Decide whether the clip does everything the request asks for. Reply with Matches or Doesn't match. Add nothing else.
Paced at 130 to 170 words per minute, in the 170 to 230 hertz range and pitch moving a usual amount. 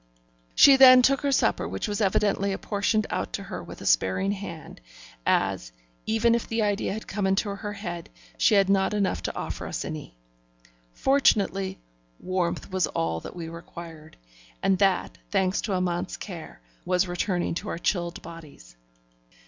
Matches